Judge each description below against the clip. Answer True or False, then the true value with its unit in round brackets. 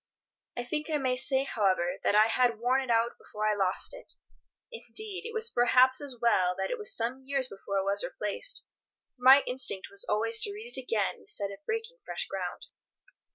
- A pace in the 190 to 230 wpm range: True (200 wpm)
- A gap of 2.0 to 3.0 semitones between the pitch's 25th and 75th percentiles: False (5.4 semitones)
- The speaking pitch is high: True (250 Hz)